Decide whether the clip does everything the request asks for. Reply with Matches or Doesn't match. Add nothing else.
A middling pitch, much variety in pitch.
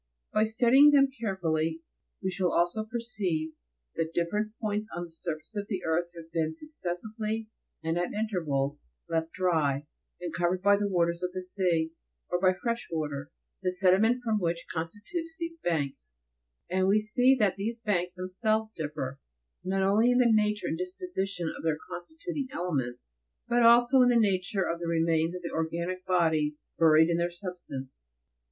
Doesn't match